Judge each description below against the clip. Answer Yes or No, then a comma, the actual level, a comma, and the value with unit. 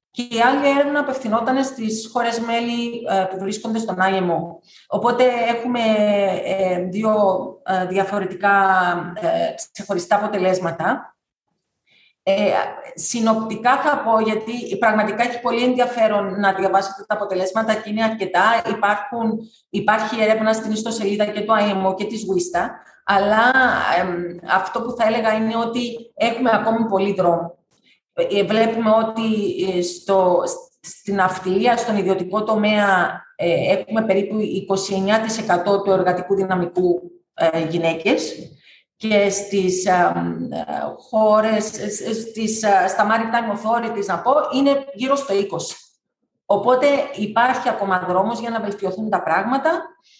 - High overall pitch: Yes, high, 215 Hz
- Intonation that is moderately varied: Yes, average, 3.3 semitones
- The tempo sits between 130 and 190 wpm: No, slow, 115 wpm